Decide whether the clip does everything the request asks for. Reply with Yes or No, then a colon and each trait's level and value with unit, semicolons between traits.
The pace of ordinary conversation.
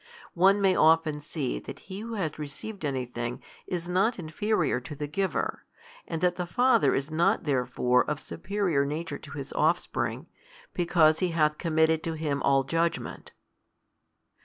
Yes: average, 155 wpm